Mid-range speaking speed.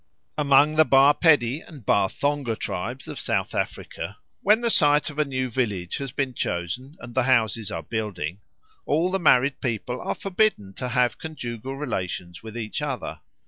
Yes: average, 175 wpm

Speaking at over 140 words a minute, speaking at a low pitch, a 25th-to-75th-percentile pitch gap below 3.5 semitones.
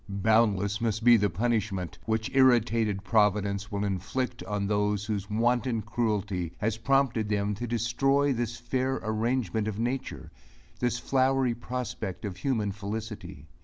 No: slow, 135 wpm; low, 110 Hz; average, 2.9 semitones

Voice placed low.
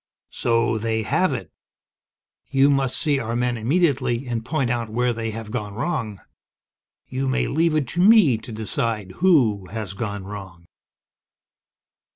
Yes: low, 115 Hz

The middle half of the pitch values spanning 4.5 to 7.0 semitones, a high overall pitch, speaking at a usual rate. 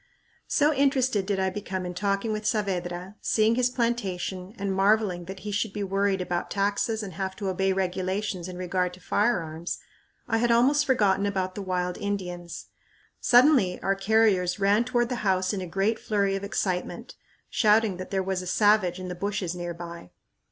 No: average, 2.7 semitones; high, 195 Hz; average, 180 wpm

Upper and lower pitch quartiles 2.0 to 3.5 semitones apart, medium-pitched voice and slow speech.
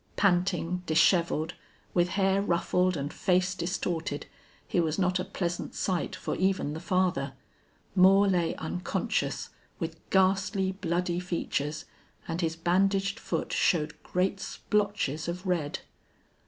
Yes: narrow, 2.4 semitones; medium, 180 Hz; slow, 125 wpm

